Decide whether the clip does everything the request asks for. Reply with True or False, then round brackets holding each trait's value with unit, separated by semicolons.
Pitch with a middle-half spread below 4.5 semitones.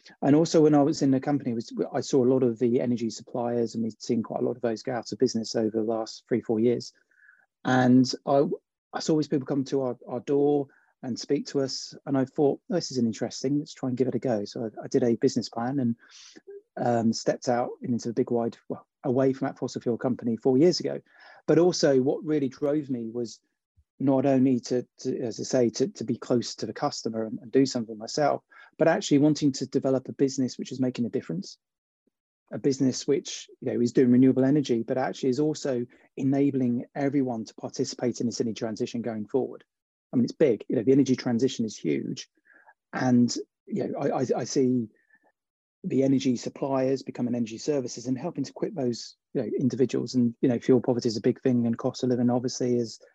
True (2.5 semitones)